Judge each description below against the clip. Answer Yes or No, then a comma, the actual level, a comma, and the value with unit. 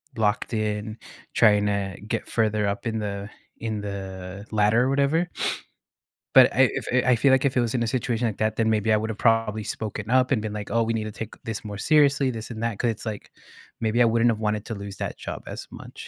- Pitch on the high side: No, low, 110 Hz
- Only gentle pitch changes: Yes, narrow, 2.0 semitones